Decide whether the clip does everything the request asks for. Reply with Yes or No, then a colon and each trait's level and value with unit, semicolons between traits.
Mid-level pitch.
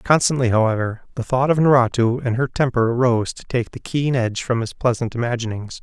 No: low, 120 Hz